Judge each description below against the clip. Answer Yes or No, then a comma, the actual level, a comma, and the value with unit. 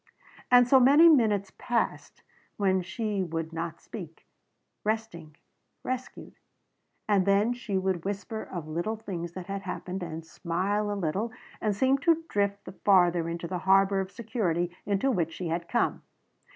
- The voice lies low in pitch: No, high, 195 Hz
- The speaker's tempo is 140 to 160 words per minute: Yes, average, 155 wpm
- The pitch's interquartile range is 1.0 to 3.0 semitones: No, average, 4.1 semitones